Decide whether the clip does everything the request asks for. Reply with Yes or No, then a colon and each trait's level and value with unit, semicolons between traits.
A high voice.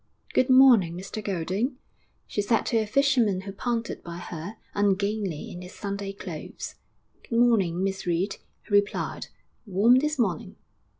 Yes: high, 205 Hz